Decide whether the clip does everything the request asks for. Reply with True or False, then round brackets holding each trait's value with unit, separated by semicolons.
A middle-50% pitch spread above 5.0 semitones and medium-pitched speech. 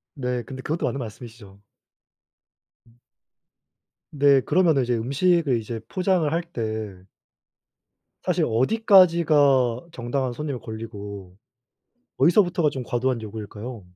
False (5.5 semitones; 130 Hz)